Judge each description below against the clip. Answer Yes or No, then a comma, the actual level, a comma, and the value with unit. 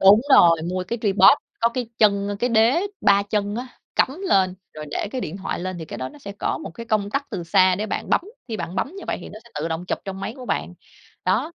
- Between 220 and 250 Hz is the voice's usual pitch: No, high, 200 Hz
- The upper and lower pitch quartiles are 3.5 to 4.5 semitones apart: Yes, average, 3.8 semitones